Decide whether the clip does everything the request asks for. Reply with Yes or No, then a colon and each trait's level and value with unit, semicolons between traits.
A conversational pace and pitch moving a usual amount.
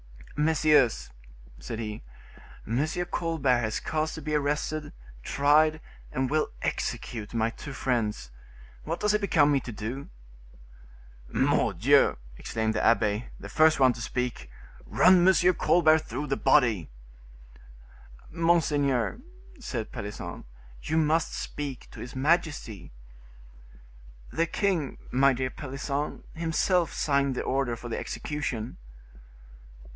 No: slow, 120 wpm; average, 4.8 semitones